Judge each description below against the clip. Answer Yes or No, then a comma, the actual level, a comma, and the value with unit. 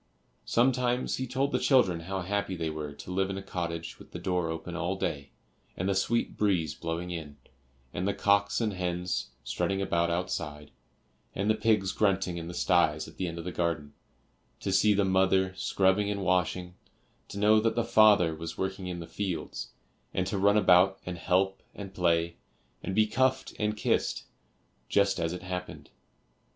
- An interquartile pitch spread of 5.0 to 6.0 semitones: No, average, 3.0 semitones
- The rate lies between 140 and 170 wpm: No, average, 185 wpm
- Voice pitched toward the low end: Yes, very low, 95 Hz